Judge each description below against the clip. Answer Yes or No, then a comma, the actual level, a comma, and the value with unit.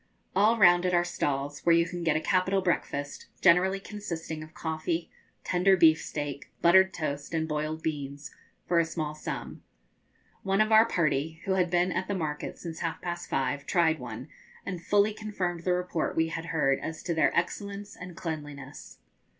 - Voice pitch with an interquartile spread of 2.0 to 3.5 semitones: Yes, average, 3.0 semitones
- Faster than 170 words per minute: Yes, average, 180 wpm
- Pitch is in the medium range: Yes, medium, 170 Hz